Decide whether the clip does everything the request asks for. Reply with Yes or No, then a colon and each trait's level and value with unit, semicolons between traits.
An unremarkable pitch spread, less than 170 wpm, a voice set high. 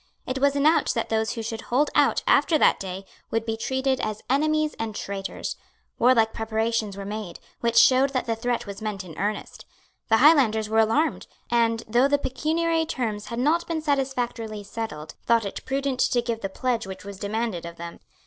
No: average, 3.8 semitones; average, 190 wpm; high, 230 Hz